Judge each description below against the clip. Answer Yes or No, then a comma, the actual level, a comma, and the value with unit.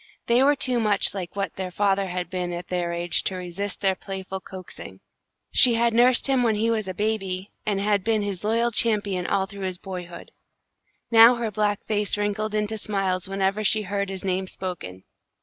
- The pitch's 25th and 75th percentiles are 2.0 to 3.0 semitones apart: Yes, narrow, 2.6 semitones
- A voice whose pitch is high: Yes, high, 200 Hz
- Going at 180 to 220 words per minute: Yes, average, 195 wpm